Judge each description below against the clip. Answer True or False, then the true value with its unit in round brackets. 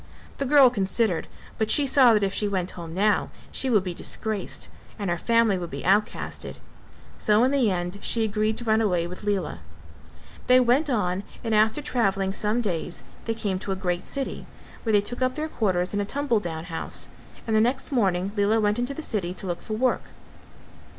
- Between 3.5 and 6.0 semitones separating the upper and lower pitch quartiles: True (4.1 semitones)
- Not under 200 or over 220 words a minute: True (205 wpm)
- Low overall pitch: False (210 Hz)